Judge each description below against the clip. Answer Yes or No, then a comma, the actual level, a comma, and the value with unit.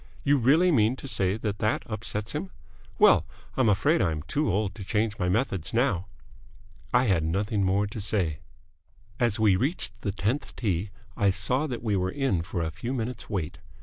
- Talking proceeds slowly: No, average, 190 wpm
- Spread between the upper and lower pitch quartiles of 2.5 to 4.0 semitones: No, average, 4.6 semitones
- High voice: No, low, 105 Hz